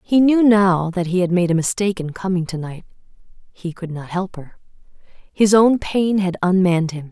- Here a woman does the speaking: Yes, female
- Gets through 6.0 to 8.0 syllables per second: No, 5.1 syllables/s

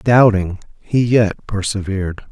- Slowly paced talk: Yes, slow, 105 wpm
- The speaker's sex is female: No, male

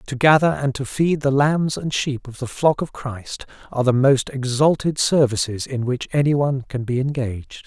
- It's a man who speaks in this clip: Yes, male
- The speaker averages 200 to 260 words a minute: Yes, fast, 205 wpm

